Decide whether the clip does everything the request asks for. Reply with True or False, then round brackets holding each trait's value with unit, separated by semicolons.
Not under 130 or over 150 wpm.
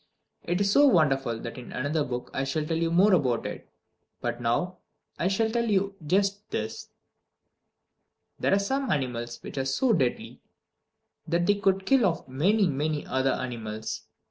False (170 wpm)